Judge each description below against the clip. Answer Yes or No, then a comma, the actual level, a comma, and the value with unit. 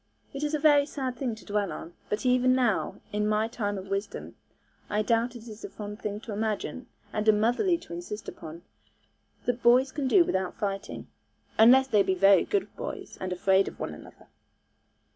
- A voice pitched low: No, high, 220 Hz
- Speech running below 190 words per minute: No, average, 195 wpm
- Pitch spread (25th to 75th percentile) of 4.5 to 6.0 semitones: No, average, 4.1 semitones